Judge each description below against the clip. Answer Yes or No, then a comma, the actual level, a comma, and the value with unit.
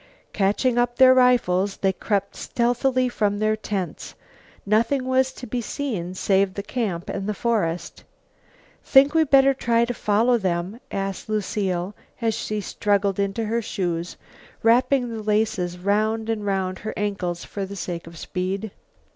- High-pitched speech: Yes, high, 210 Hz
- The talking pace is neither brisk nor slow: Yes, average, 155 wpm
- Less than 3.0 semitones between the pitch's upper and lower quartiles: No, average, 3.7 semitones